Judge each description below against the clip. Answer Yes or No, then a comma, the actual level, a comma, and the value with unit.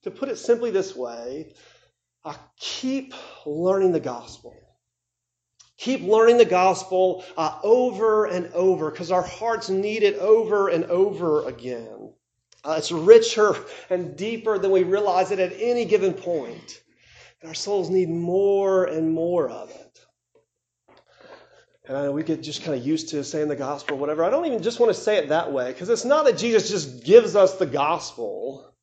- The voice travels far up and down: Yes, wide, 6.0 semitones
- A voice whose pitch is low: No, high, 190 Hz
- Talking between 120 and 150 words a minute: No, average, 175 wpm